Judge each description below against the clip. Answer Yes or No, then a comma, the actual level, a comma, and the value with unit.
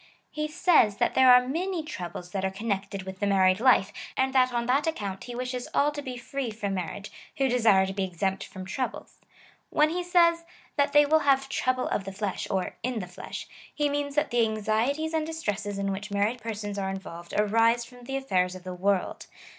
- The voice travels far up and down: Yes, wide, 5.8 semitones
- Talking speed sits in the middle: No, fast, 215 wpm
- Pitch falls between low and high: No, high, 230 Hz